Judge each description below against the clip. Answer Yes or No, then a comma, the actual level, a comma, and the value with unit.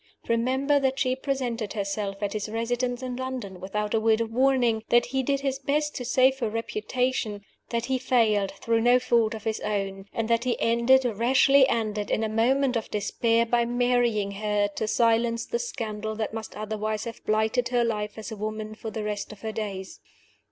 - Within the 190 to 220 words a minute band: Yes, average, 195 wpm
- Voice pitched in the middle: No, high, 230 Hz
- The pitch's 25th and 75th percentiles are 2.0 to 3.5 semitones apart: Yes, average, 2.8 semitones